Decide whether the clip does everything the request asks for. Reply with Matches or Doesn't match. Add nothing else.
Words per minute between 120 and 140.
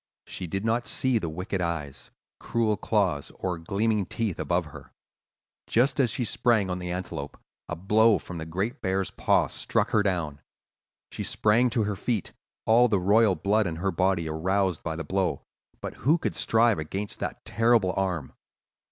Doesn't match